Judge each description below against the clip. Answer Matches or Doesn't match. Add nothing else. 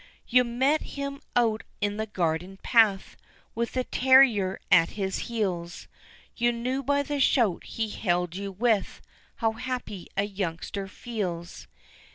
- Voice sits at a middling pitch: Doesn't match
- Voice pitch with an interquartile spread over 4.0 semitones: Matches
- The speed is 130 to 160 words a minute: Matches